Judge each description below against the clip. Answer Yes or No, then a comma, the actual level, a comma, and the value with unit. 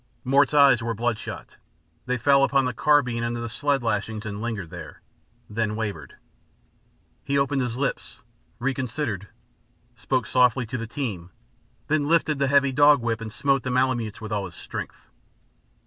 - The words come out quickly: No, average, 160 wpm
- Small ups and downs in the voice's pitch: No, average, 3.6 semitones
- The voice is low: Yes, low, 125 Hz